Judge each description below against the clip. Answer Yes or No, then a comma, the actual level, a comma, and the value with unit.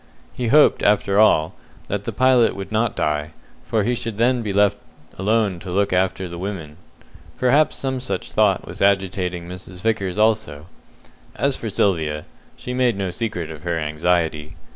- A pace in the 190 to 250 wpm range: No, average, 165 wpm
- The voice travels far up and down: No, average, 4.5 semitones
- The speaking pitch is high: No, low, 100 Hz